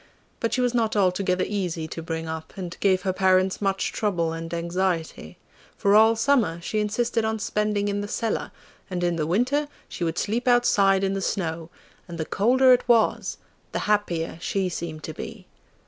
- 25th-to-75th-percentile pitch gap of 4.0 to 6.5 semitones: Yes, average, 4.3 semitones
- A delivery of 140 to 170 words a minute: No, average, 185 wpm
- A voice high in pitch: Yes, high, 195 Hz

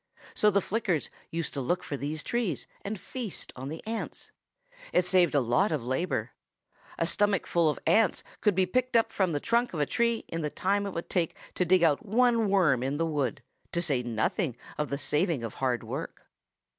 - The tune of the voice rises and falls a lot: Yes, wide, 5.9 semitones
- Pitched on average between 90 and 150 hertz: No, medium, 170 Hz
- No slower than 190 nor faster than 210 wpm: Yes, average, 200 wpm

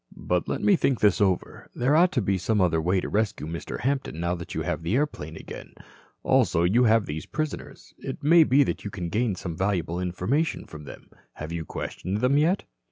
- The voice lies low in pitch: Yes, low, 100 Hz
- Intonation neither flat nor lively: No, wide, 7.4 semitones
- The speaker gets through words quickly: Yes, fast, 215 wpm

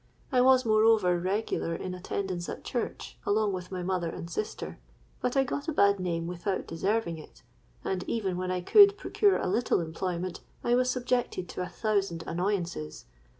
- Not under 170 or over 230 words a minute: Yes, average, 175 wpm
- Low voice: No, high, 190 Hz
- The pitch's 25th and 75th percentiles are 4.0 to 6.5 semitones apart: Yes, average, 4.3 semitones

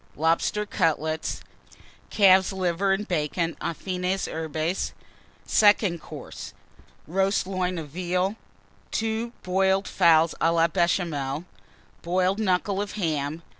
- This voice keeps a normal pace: No, slow, 110 wpm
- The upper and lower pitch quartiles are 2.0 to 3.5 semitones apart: Yes, average, 2.8 semitones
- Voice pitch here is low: No, medium, 180 Hz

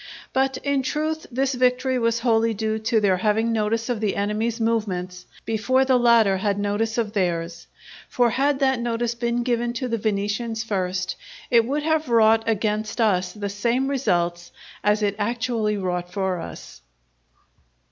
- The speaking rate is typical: Yes, average, 160 wpm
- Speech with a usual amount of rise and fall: Yes, average, 3.0 semitones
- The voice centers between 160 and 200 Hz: No, high, 225 Hz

